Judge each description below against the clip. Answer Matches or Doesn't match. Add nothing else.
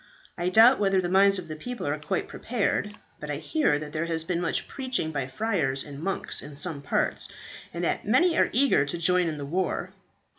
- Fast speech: Matches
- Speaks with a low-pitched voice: Doesn't match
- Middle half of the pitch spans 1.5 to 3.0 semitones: Doesn't match